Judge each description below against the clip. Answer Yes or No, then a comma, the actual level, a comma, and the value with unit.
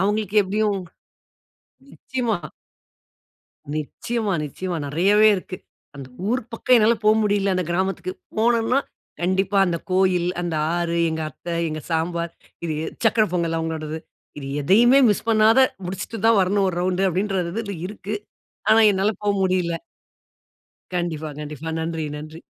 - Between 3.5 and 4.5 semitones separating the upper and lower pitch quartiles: Yes, average, 4.0 semitones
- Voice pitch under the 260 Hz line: Yes, high, 190 Hz